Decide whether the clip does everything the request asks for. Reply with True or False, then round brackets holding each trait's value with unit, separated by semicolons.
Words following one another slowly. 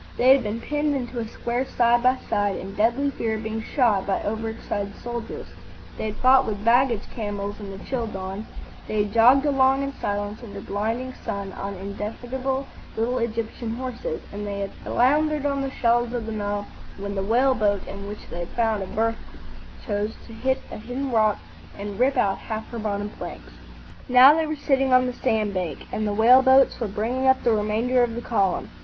False (205 wpm)